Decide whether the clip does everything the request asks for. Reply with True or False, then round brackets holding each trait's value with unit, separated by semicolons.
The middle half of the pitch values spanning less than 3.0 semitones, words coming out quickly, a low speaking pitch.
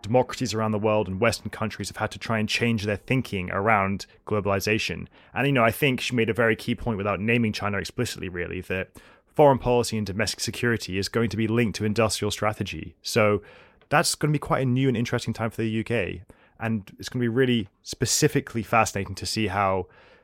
True (2.6 semitones; 215 wpm; 110 Hz)